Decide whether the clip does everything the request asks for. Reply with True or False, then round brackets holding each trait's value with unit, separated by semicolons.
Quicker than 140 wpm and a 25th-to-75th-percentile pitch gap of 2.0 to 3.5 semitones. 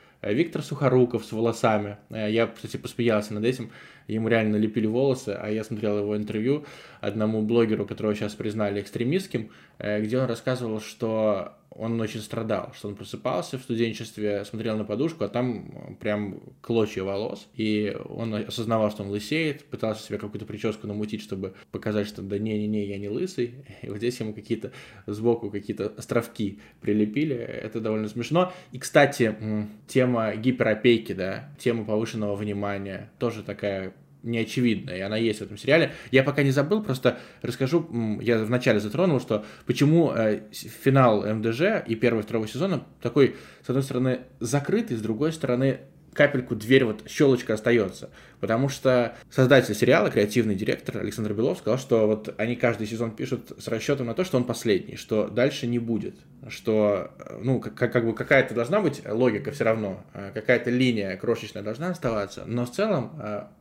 True (160 wpm; 3.1 semitones)